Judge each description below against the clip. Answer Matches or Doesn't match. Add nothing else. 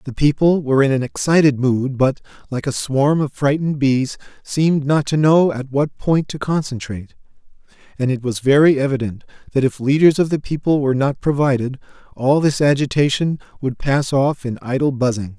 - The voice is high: Doesn't match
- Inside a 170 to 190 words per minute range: Matches